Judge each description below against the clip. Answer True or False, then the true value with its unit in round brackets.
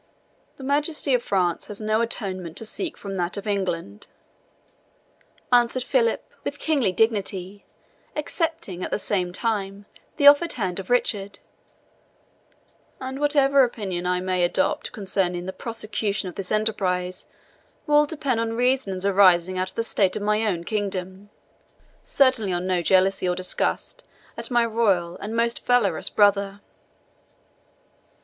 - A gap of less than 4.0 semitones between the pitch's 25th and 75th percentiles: False (4.4 semitones)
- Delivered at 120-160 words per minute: True (140 wpm)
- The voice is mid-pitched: False (205 Hz)